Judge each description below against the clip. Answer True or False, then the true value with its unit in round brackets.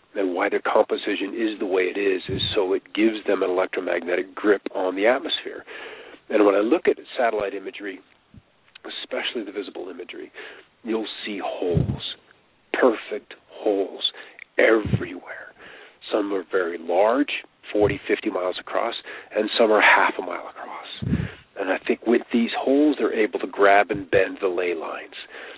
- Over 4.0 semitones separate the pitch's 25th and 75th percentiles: True (4.6 semitones)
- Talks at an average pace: True (155 wpm)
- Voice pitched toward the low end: False (390 Hz)